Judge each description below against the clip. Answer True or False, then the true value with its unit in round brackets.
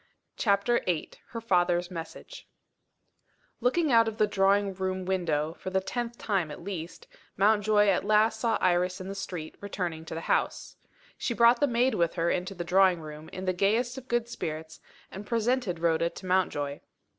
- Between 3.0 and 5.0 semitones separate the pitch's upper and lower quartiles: True (4.1 semitones)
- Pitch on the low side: False (190 Hz)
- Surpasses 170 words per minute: True (180 wpm)